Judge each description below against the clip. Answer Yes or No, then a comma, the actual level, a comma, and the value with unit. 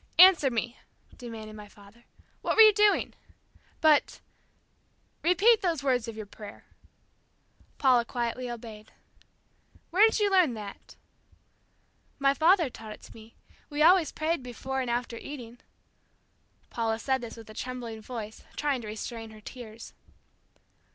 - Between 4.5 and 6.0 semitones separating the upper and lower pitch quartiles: Yes, average, 5.2 semitones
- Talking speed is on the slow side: No, average, 145 wpm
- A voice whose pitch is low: No, high, 245 Hz